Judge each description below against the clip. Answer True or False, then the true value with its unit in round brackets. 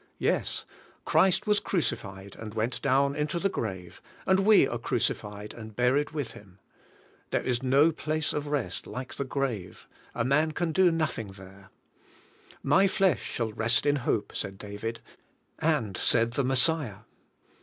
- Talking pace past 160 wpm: False (155 wpm)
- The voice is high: False (130 Hz)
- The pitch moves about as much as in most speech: False (5.9 semitones)